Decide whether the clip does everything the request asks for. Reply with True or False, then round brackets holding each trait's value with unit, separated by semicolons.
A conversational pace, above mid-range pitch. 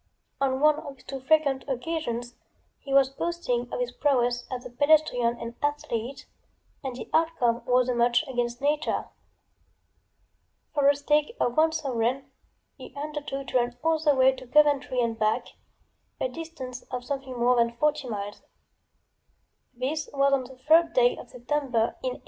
True (165 wpm; 265 Hz)